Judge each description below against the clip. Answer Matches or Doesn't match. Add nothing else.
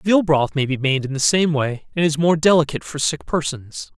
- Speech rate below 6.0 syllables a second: Matches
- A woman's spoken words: Doesn't match